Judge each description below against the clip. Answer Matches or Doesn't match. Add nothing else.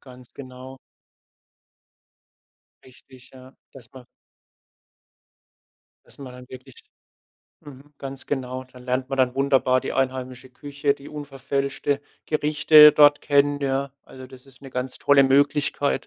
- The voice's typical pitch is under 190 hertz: Matches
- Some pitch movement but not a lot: Doesn't match